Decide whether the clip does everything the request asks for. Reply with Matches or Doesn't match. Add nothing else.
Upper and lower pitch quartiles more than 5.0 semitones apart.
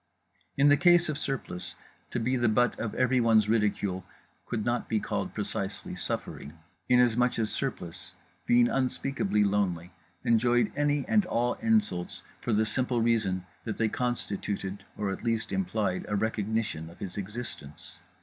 Doesn't match